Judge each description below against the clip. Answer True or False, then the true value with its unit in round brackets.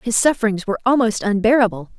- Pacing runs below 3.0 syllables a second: False (6.8 syllables/s)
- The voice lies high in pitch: True (220 Hz)